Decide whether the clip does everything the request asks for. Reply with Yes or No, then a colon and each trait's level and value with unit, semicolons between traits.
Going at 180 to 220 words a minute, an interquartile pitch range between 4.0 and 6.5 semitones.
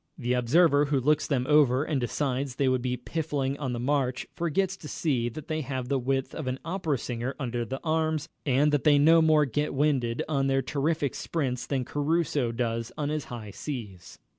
No: average, 200 wpm; average, 3.3 semitones